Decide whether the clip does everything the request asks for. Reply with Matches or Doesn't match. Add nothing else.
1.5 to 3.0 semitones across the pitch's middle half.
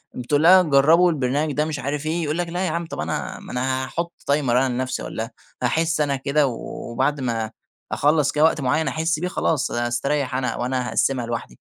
Doesn't match